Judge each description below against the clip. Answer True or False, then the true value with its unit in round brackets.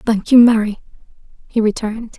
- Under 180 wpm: True (135 wpm)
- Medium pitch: False (220 Hz)